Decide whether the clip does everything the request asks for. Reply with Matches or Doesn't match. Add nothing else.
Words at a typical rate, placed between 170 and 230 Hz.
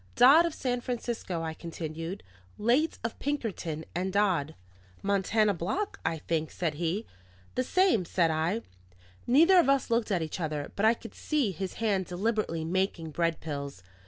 Matches